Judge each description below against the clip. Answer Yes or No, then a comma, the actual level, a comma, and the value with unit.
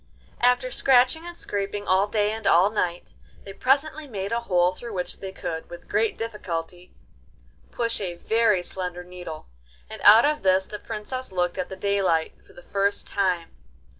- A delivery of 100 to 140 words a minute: No, average, 170 wpm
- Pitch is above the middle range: Yes, high, 200 Hz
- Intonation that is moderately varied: Yes, average, 4.2 semitones